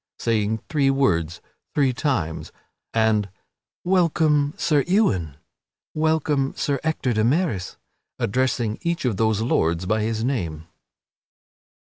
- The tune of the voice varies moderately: No, wide, 5.9 semitones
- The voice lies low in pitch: Yes, low, 125 Hz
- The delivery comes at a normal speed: No, slow, 110 wpm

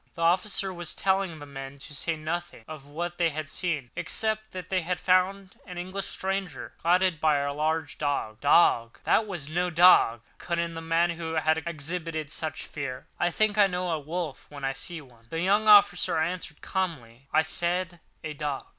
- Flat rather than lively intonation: No, average, 3.6 semitones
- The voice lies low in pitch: No, medium, 165 Hz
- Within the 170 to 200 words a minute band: Yes, average, 190 wpm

